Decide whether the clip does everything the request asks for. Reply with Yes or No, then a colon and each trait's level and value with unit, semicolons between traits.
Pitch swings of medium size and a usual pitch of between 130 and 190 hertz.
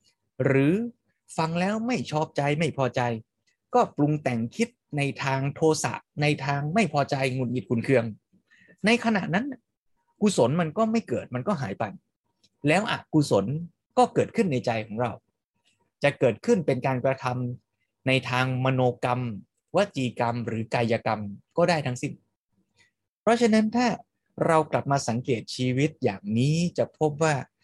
No: wide, 5.7 semitones; medium, 140 Hz